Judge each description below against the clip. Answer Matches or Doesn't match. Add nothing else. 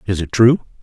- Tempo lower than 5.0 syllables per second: Doesn't match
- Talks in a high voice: Doesn't match